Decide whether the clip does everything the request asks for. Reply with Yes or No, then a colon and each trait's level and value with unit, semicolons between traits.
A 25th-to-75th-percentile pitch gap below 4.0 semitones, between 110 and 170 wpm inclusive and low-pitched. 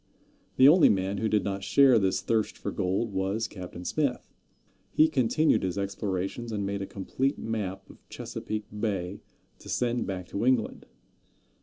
Yes: average, 3.6 semitones; average, 160 wpm; low, 105 Hz